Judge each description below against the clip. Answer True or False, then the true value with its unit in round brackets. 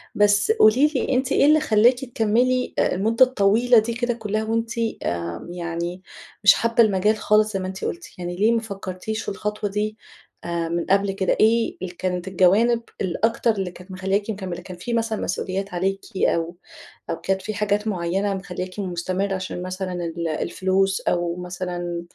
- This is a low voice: False (195 Hz)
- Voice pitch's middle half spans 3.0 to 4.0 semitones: True (3.5 semitones)